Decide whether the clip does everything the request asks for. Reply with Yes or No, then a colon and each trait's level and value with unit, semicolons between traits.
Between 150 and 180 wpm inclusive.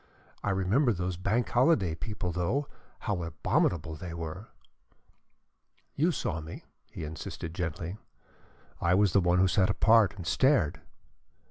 No: slow, 135 wpm